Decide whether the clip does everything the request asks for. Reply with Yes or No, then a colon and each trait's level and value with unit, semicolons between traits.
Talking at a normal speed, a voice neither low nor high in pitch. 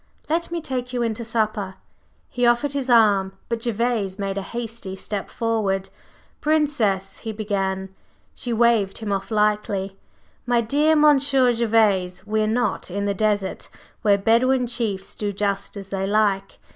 No: average, 160 wpm; high, 215 Hz